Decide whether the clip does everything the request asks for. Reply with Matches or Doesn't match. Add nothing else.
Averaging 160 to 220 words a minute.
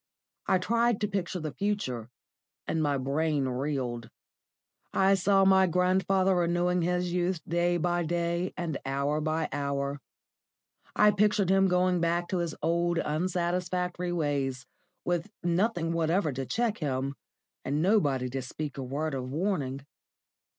Doesn't match